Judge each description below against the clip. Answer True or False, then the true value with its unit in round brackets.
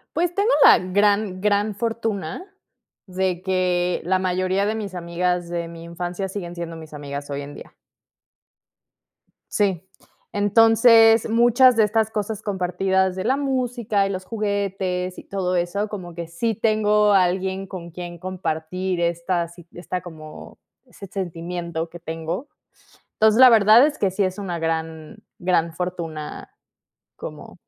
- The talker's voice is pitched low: False (185 Hz)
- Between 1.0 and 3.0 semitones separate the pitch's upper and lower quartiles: False (3.4 semitones)